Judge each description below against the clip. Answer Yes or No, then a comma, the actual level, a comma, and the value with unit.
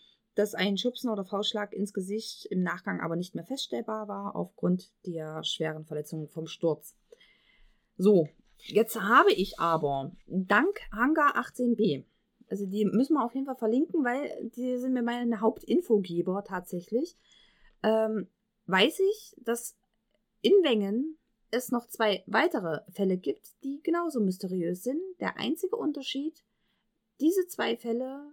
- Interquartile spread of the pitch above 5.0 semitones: Yes, wide, 5.5 semitones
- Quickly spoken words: No, average, 140 wpm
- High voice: Yes, high, 220 Hz